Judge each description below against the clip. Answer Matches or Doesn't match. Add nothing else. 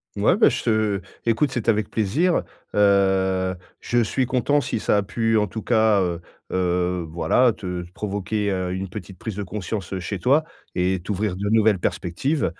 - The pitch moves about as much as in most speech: Matches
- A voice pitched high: Doesn't match